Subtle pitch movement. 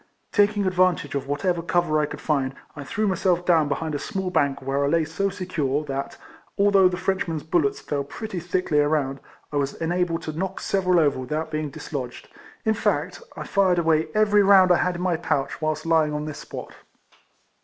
No: average, 3.9 semitones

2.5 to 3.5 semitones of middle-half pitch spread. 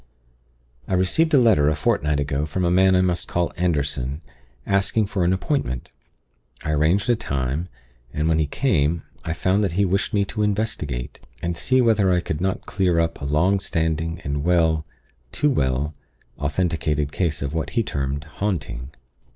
No: average, 4.6 semitones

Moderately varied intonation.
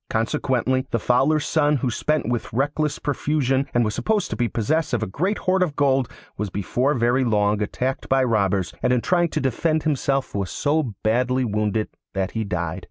Yes: average, 5.0 semitones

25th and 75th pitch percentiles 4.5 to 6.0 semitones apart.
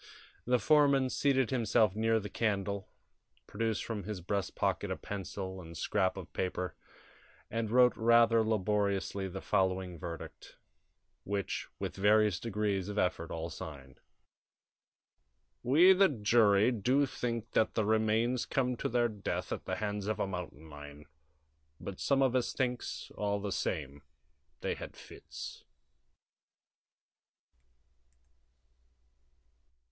No: average, 3.8 semitones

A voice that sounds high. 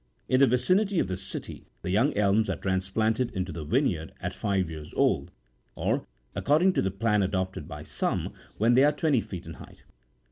No: low, 105 Hz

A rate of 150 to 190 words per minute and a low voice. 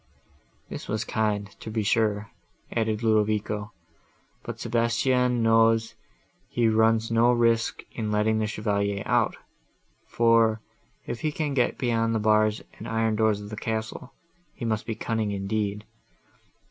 No: average, 140 wpm; low, 110 Hz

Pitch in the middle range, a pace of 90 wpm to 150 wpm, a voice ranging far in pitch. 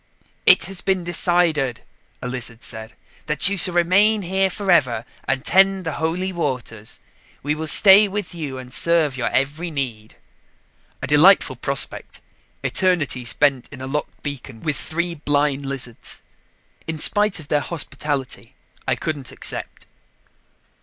No: medium, 150 Hz; average, 140 wpm; average, 5.0 semitones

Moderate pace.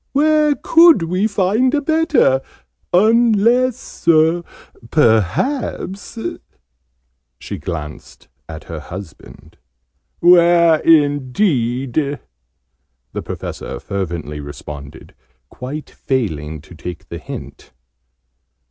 No: slow, 85 wpm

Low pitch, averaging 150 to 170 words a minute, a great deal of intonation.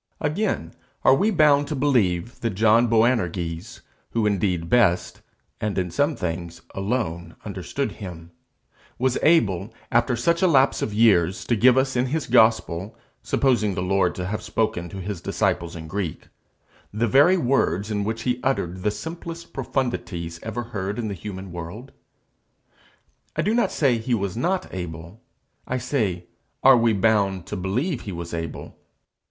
Yes: low, 105 Hz; average, 160 wpm; wide, 5.9 semitones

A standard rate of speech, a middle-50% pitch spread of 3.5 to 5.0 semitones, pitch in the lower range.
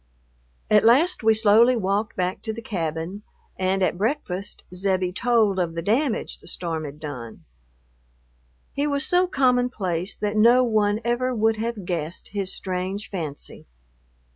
No: average, 150 wpm; average, 4.4 semitones; high, 205 Hz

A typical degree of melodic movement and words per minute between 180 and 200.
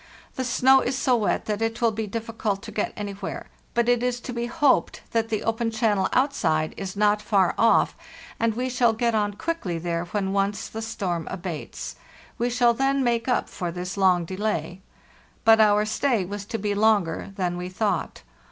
Yes: average, 3.4 semitones; average, 190 wpm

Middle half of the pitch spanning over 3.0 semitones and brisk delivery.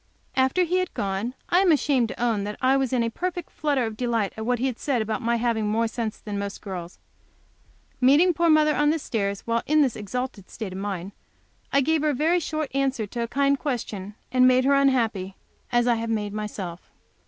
Yes: average, 4.7 semitones; fast, 220 wpm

